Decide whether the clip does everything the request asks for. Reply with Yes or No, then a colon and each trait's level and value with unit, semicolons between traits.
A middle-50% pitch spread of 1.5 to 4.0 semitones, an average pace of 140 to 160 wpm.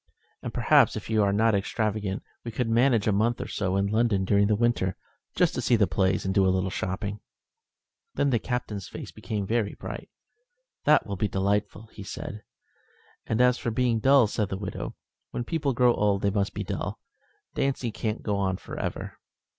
No: average, 3.0 semitones; average, 195 wpm